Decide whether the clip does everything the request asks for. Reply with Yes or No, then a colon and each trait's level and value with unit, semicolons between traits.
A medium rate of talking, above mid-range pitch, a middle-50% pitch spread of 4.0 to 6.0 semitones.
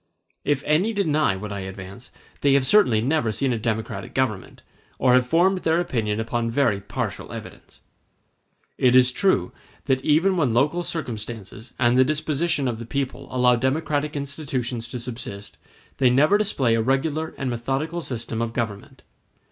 No: average, 160 wpm; low, 130 Hz; average, 4.8 semitones